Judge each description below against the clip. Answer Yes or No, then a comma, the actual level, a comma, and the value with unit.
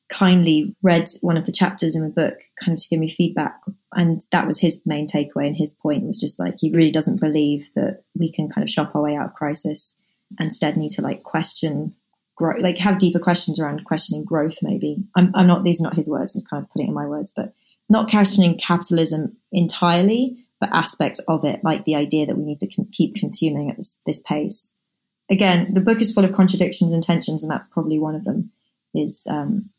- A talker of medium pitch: Yes, medium, 175 Hz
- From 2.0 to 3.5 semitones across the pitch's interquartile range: No, average, 4.0 semitones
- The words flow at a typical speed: No, fast, 225 wpm